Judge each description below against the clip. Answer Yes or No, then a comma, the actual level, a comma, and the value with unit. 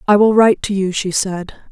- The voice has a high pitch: Yes, high, 200 Hz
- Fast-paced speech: Yes, fast, 245 wpm